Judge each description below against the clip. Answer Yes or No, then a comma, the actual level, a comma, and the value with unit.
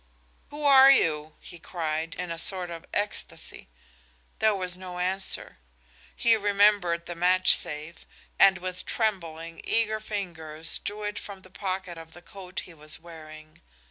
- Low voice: No, medium, 180 Hz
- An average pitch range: Yes, average, 3.5 semitones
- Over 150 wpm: No, average, 145 wpm